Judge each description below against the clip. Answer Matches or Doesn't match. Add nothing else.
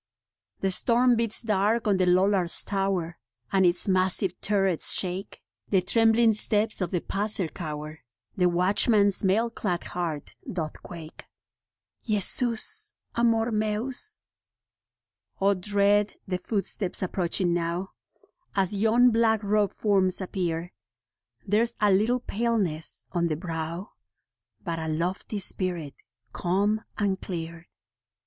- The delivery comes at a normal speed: Doesn't match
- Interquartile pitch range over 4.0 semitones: Doesn't match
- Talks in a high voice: Matches